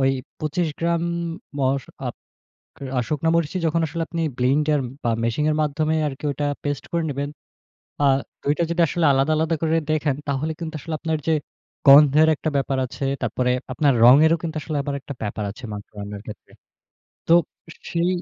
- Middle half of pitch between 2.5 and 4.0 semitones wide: Yes, average, 3.0 semitones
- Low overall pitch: No, medium, 150 Hz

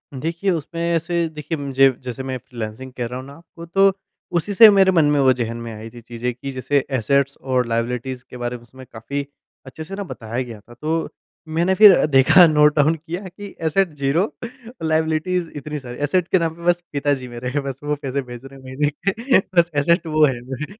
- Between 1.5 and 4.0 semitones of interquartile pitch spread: No, average, 4.7 semitones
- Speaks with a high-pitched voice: No, medium, 145 Hz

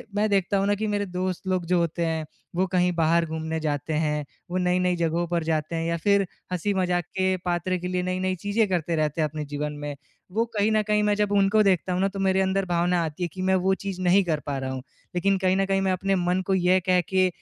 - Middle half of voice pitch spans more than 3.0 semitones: No, narrow, 2.5 semitones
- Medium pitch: Yes, medium, 180 Hz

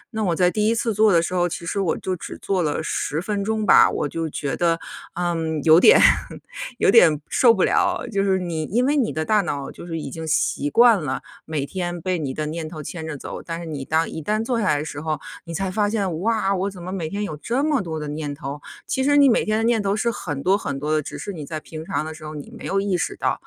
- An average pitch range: Yes, average, 4.7 semitones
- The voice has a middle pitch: Yes, medium, 175 Hz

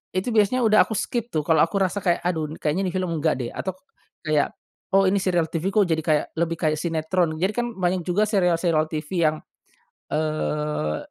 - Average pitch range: Yes, average, 3.6 semitones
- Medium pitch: Yes, medium, 170 Hz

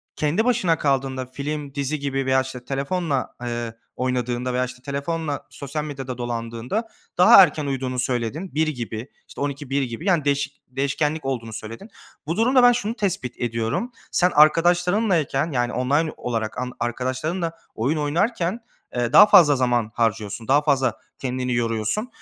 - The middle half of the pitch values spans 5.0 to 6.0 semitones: No, average, 4.4 semitones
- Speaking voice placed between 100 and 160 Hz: Yes, low, 135 Hz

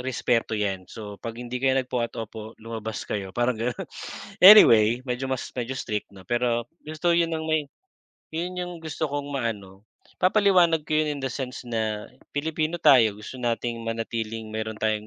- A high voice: No, low, 120 Hz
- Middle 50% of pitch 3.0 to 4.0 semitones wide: No, average, 5.3 semitones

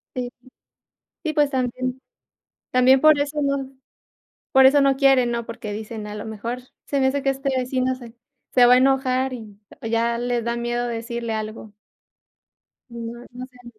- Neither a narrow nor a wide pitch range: No, narrow, 2.2 semitones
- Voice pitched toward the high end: Yes, very high, 250 Hz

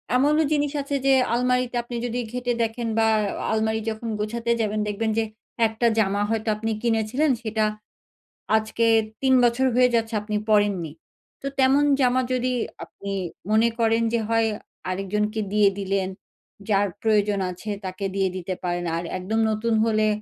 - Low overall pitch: No, high, 220 Hz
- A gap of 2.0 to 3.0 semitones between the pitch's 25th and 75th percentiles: Yes, average, 2.7 semitones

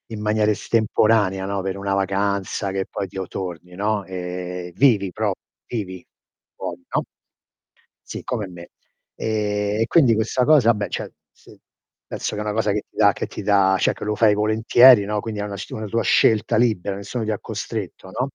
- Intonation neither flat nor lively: No, narrow, 2.2 semitones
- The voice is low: Yes, low, 105 Hz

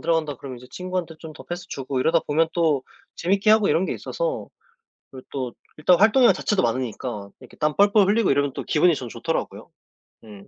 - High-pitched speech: No, medium, 160 Hz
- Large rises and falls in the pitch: Yes, wide, 6.0 semitones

